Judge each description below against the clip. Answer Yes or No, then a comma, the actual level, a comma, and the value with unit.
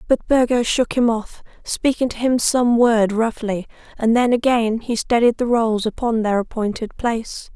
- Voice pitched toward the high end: Yes, high, 230 Hz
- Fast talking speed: No, average, 175 wpm